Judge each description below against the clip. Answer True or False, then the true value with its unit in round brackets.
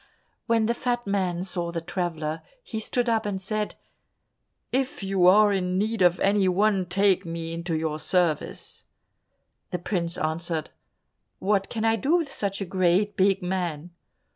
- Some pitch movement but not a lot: True (3.5 semitones)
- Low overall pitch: False (190 Hz)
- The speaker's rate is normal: True (160 wpm)